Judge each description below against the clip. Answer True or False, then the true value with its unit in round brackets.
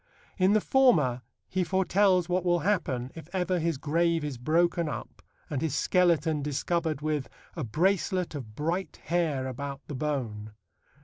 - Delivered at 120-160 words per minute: True (150 wpm)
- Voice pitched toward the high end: False (160 Hz)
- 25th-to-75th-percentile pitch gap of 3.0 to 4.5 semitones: True (4.1 semitones)